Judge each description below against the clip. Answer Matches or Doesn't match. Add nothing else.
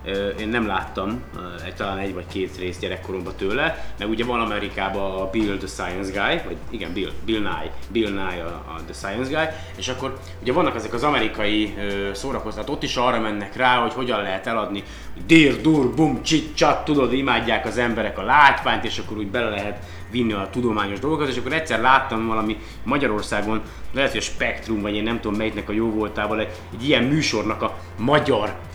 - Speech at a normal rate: Doesn't match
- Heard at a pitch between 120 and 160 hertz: Doesn't match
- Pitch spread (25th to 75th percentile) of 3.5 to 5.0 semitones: Matches